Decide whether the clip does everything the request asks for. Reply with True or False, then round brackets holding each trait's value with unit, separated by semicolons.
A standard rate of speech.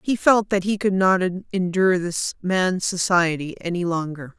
True (165 wpm)